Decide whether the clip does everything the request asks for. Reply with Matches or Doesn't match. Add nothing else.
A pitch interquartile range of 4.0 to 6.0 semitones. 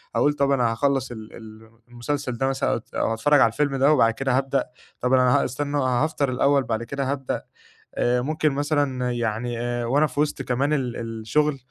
Doesn't match